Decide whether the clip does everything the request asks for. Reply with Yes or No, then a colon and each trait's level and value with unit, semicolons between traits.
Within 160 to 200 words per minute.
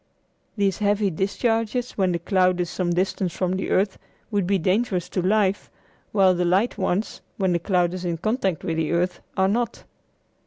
Yes: average, 185 wpm